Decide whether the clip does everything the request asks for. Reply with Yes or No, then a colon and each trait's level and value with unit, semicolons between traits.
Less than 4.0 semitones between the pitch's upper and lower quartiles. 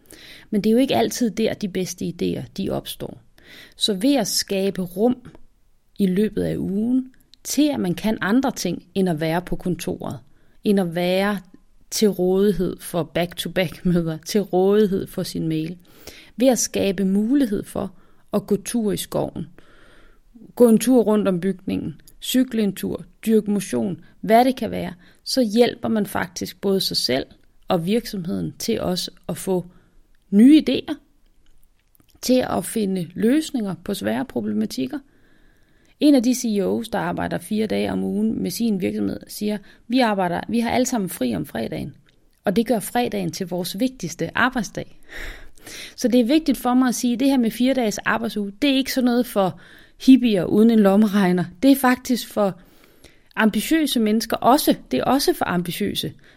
No: average, 4.6 semitones